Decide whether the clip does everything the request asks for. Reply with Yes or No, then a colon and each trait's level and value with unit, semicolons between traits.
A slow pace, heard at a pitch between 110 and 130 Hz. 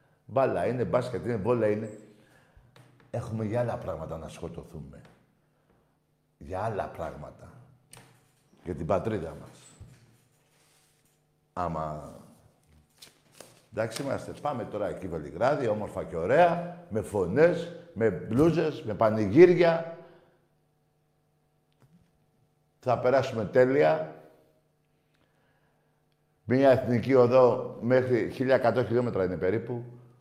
Yes: slow, 90 wpm; low, 125 Hz